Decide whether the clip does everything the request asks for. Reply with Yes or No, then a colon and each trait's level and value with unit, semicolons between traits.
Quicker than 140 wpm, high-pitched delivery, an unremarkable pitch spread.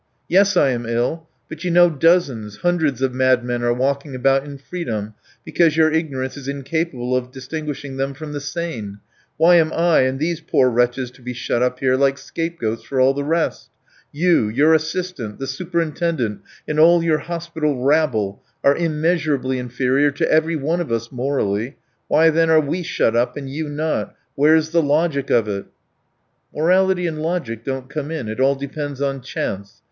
No: average, 180 wpm; medium, 140 Hz; average, 4.0 semitones